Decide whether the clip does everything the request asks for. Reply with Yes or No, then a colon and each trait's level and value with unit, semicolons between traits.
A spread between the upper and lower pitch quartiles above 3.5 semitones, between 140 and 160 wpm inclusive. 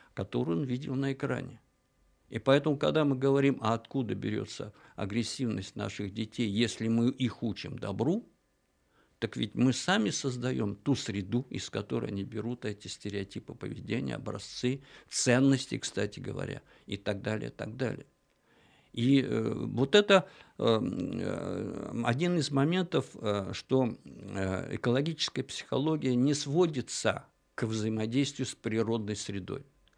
No: average, 4.4 semitones; average, 120 wpm